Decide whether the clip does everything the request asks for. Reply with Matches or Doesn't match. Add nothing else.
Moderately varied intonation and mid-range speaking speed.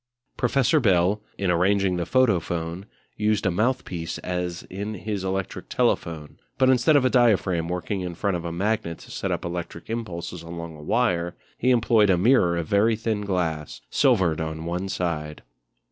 Matches